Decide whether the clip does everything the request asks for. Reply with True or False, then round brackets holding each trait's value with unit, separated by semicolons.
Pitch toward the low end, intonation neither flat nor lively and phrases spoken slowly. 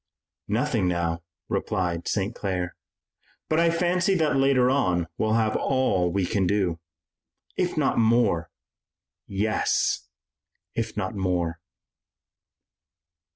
False (105 Hz; 6.3 semitones; 110 wpm)